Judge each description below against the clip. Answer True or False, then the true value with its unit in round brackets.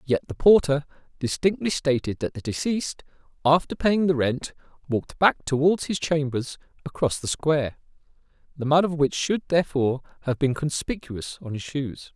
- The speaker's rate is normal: True (160 wpm)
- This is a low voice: False (150 Hz)